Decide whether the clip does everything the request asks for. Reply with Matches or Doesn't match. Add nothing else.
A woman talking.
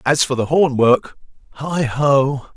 Doesn't match